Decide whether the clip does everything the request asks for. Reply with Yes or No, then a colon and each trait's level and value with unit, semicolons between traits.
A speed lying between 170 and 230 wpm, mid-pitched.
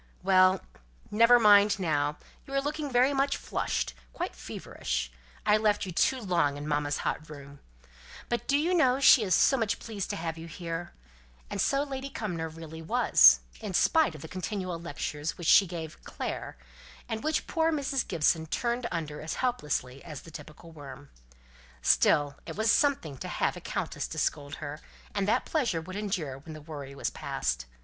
Yes: average, 180 wpm; medium, 180 Hz